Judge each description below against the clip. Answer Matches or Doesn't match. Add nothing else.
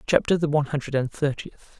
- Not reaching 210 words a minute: Matches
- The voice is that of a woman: Doesn't match